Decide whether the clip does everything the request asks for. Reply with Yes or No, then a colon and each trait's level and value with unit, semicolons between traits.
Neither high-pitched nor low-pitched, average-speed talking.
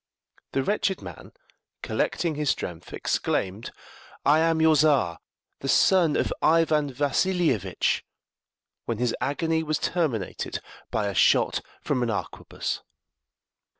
No: medium, 145 Hz; slow, 115 wpm